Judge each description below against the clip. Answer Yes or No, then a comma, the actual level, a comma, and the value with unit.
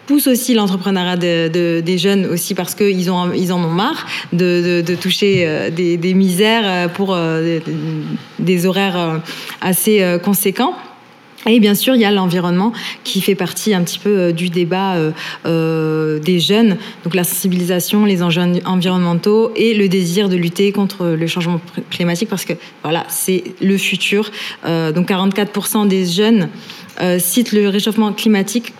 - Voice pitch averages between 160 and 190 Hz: Yes, medium, 185 Hz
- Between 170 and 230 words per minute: No, average, 155 wpm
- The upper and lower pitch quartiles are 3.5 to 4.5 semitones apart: No, average, 2.8 semitones